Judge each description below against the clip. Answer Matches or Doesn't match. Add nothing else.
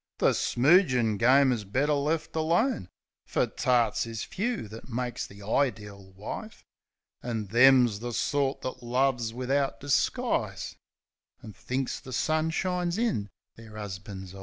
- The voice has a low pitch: Matches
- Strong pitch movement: Doesn't match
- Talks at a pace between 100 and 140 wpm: Matches